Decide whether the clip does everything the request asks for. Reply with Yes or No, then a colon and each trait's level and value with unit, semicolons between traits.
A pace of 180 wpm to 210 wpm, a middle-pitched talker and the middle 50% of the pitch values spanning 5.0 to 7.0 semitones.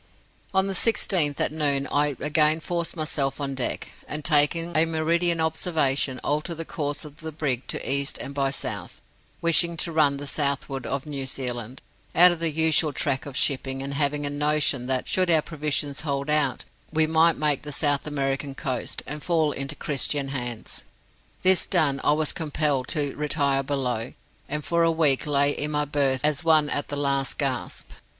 No: average, 185 wpm; medium, 145 Hz; narrow, 2.4 semitones